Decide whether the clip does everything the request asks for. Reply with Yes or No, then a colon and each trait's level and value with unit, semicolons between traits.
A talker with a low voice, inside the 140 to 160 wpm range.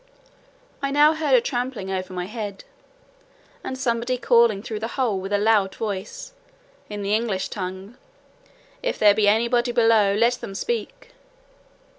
No: high, 225 Hz; average, 155 wpm